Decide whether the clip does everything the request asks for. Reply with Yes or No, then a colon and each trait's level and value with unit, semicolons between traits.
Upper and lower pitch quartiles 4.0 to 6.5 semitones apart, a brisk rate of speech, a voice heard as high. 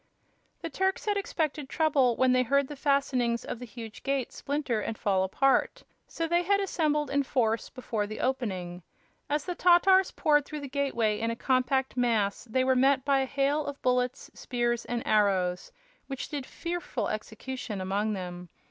No: average, 4.3 semitones; average, 175 wpm; very high, 260 Hz